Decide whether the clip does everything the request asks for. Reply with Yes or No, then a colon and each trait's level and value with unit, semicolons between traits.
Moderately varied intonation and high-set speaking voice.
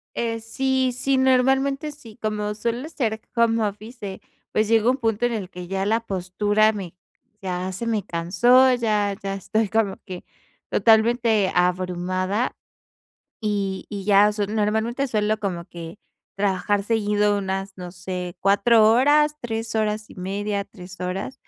Yes: average, 3.2 semitones; high, 210 Hz